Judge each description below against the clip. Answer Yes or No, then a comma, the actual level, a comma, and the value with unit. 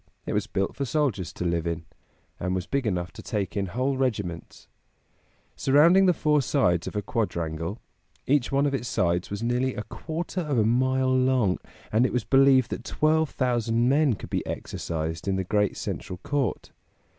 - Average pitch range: No, wide, 6.3 semitones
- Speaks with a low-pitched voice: Yes, low, 120 Hz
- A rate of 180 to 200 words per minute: Yes, average, 185 wpm